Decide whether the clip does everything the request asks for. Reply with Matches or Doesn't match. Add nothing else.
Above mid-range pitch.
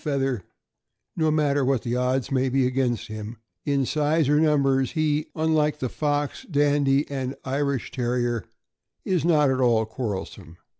Doesn't match